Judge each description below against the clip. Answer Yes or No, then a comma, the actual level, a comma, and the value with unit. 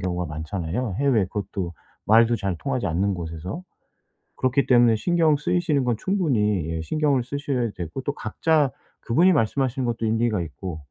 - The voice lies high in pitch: No, low, 115 Hz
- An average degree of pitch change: No, wide, 7.0 semitones